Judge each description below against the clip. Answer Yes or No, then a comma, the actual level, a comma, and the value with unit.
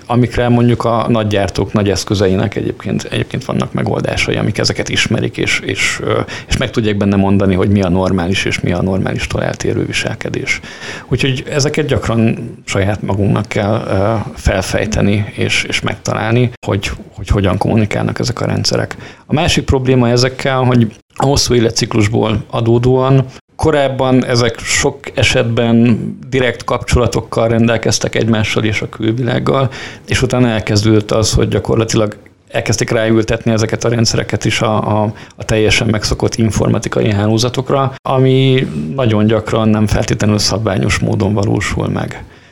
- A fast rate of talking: No, average, 135 wpm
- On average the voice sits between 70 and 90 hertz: No, low, 115 Hz